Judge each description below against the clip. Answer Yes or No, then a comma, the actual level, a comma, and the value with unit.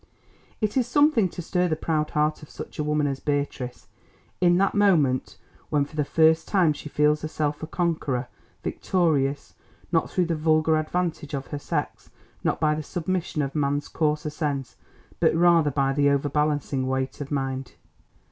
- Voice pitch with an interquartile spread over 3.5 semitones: No, average, 2.7 semitones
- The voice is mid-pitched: Yes, medium, 150 Hz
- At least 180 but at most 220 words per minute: No, average, 170 wpm